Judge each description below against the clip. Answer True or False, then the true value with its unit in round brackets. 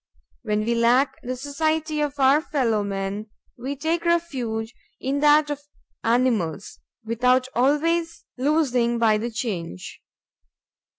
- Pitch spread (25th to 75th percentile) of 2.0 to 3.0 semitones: False (4.7 semitones)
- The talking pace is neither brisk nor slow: False (120 wpm)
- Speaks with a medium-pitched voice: False (255 Hz)